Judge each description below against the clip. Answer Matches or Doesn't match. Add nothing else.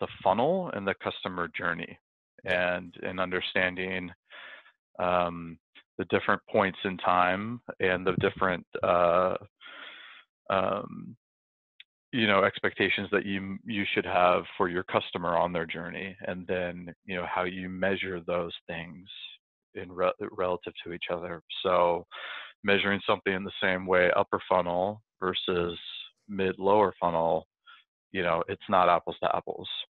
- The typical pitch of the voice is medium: Doesn't match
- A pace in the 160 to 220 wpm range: Doesn't match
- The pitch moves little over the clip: Matches